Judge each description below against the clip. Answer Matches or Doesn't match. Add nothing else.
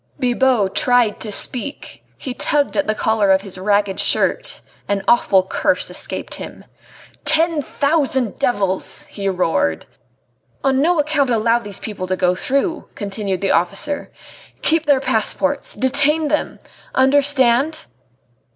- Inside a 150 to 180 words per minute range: Doesn't match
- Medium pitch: Doesn't match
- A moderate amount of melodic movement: Doesn't match